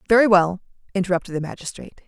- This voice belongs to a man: No, female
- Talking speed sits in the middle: Yes, average, 145 wpm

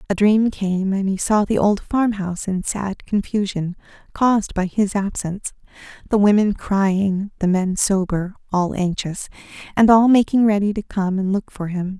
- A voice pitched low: No, high, 200 Hz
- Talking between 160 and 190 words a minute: Yes, average, 170 wpm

